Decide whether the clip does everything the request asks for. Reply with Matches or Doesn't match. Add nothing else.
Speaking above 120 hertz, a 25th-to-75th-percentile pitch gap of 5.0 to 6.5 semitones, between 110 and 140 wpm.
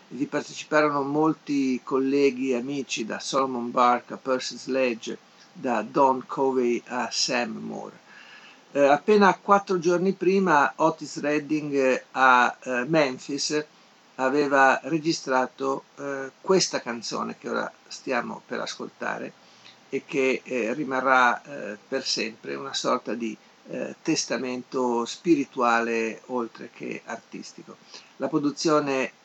Doesn't match